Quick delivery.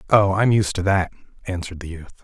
Yes: fast, 240 wpm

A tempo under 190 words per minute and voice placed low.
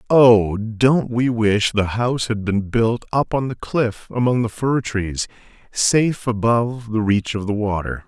Yes: average, 180 wpm; low, 115 Hz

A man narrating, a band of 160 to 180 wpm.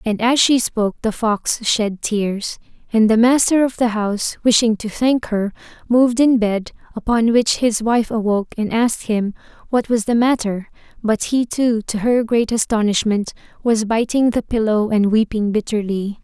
No: female; average, 175 wpm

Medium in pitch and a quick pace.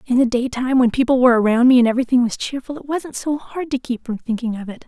No: very high, 250 Hz; fast, 270 wpm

